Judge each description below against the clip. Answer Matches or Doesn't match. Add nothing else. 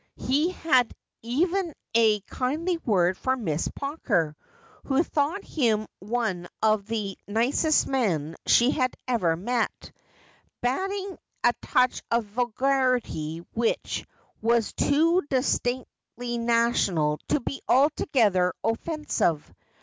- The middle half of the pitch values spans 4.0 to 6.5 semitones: Matches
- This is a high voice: Matches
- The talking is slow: Matches